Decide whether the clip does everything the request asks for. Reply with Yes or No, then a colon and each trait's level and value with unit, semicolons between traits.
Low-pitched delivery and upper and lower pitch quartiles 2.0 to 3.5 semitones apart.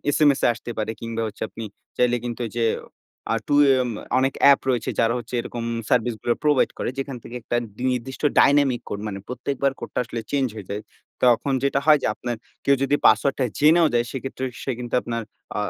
Yes: low, 125 Hz; average, 2.9 semitones